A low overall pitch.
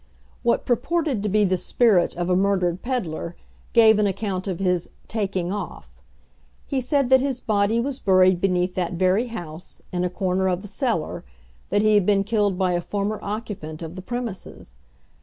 No: high, 195 Hz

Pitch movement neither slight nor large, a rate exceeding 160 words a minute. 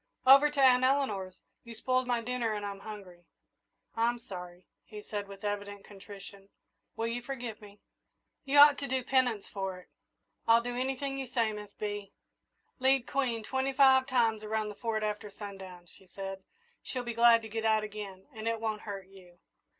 Yes: average, 3.7 semitones; average, 180 wpm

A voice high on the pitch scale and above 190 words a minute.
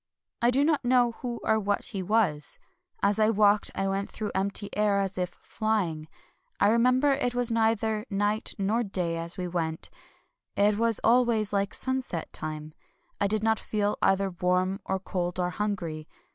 No: high, 205 Hz; average, 175 wpm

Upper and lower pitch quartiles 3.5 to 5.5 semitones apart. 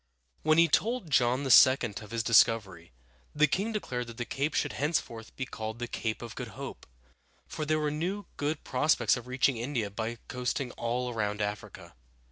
Yes: average, 4.7 semitones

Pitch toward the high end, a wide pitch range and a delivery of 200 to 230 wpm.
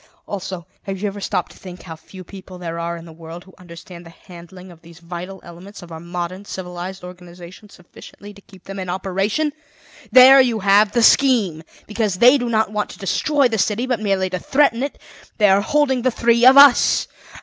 No: high, 195 Hz; average, 4.1 semitones; fast, 205 wpm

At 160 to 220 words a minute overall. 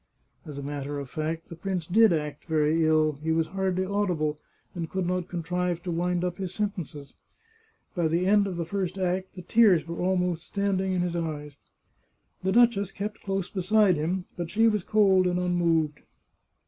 Yes: average, 185 wpm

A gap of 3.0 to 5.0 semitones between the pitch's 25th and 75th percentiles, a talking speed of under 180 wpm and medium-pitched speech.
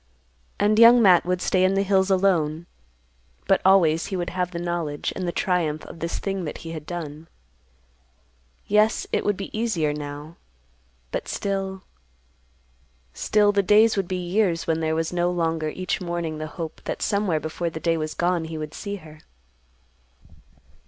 Yes: average, 3.6 semitones; average, 170 wpm; medium, 175 Hz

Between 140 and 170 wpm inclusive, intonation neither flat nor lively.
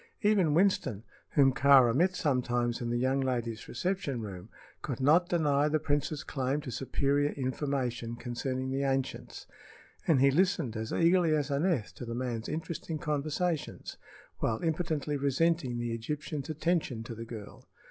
Yes: average, 150 wpm; average, 4.3 semitones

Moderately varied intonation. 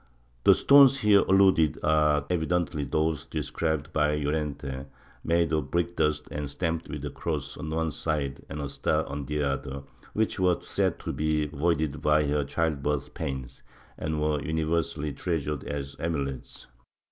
No: narrow, 2.1 semitones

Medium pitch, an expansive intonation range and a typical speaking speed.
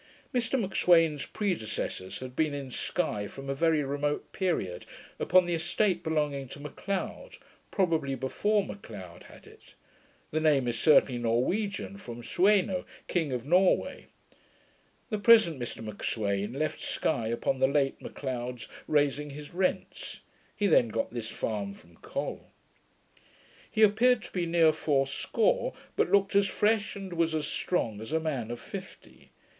Yes: medium, 150 Hz; wide, 6.9 semitones; average, 145 wpm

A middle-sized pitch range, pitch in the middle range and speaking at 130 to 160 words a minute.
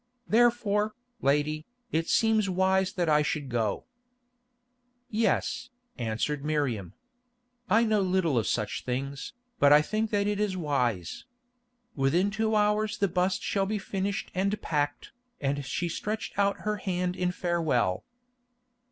No: wide, 6.2 semitones; medium, 180 Hz; slow, 135 wpm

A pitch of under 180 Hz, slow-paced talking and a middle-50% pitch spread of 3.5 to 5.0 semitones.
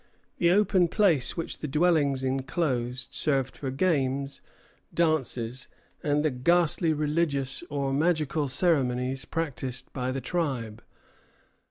Yes: medium, 140 Hz; slow, 120 wpm; average, 4.0 semitones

